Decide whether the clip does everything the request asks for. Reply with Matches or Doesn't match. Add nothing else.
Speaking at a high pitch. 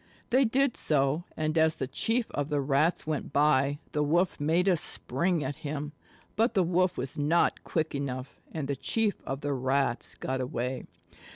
Doesn't match